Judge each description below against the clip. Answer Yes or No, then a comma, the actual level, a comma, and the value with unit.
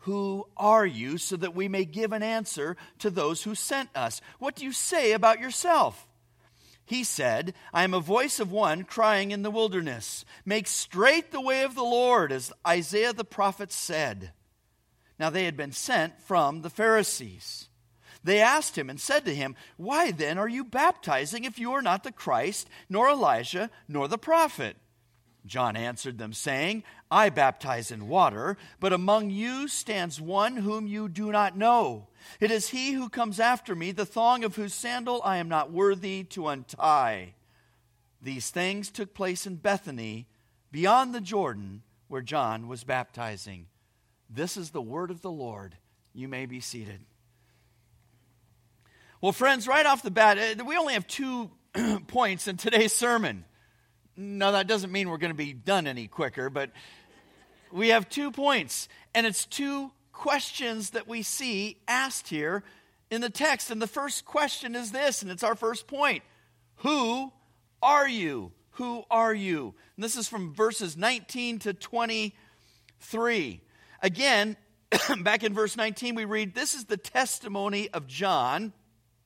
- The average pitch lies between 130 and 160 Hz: No, high, 200 Hz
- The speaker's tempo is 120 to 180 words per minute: Yes, average, 165 wpm